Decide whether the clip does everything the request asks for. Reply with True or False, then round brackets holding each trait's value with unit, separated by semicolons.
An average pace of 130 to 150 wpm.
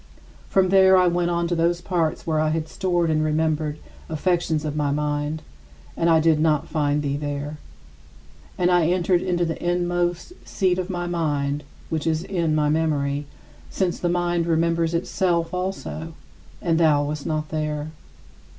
False (165 wpm)